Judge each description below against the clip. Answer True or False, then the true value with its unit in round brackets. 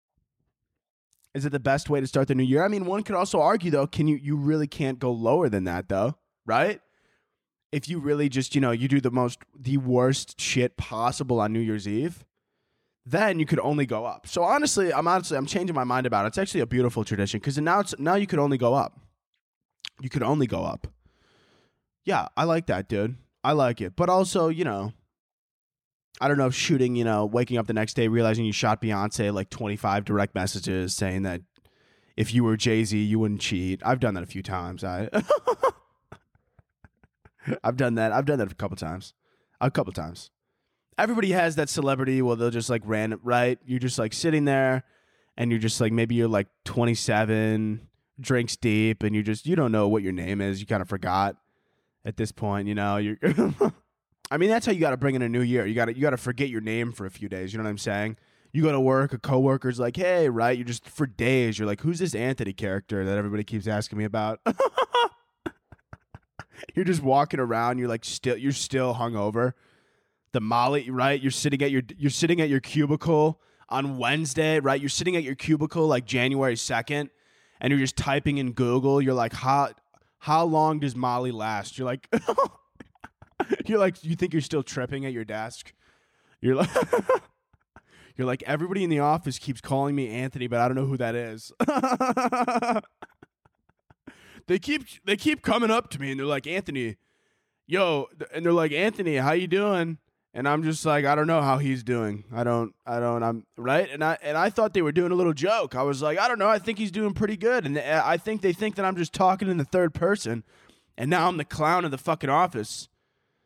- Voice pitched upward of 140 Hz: False (130 Hz)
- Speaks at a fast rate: True (210 wpm)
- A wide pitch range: True (5.7 semitones)